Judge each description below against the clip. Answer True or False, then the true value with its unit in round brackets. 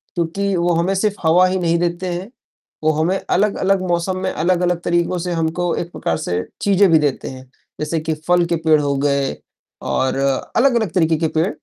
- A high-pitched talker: False (175 Hz)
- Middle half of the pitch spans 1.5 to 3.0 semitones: True (2.7 semitones)